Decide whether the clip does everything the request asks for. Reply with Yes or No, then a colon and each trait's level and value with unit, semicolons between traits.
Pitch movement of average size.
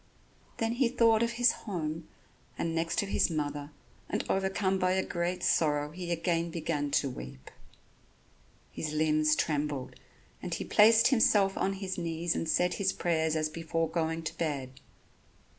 Yes: average, 3.8 semitones